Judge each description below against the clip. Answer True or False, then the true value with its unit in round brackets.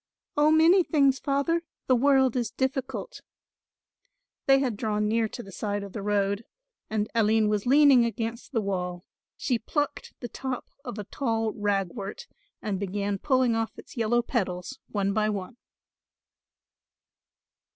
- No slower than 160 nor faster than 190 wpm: False (145 wpm)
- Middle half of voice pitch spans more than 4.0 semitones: True (4.5 semitones)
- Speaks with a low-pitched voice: False (225 Hz)